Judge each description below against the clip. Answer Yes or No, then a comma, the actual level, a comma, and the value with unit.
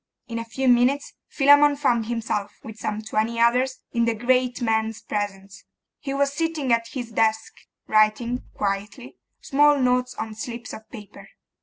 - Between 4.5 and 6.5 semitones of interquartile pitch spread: No, average, 2.9 semitones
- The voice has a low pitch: No, high, 235 Hz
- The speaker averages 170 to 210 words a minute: No, average, 155 wpm